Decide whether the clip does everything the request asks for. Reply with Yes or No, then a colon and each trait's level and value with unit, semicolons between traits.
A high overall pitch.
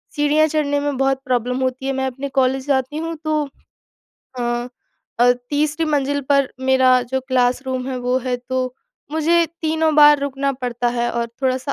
Yes: very high, 265 Hz